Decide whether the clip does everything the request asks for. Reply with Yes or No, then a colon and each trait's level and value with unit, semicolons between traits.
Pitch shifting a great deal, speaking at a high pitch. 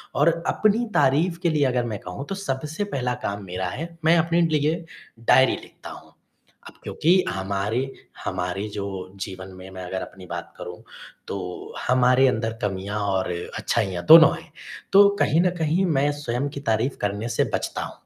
No: wide, 8.0 semitones; low, 125 Hz